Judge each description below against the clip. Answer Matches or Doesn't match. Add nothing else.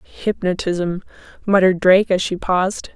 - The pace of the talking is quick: Doesn't match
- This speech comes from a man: Doesn't match